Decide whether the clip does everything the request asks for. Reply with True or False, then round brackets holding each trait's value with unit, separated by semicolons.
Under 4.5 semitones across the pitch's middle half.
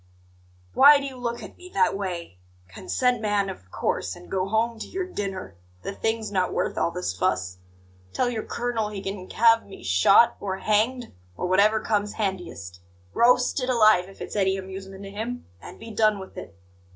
True (3.5 semitones)